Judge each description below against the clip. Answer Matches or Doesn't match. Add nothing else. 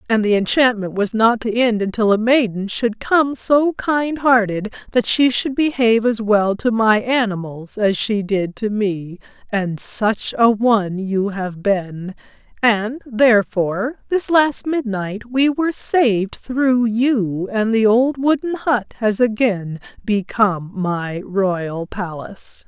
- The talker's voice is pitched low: Doesn't match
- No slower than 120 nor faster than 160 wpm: Matches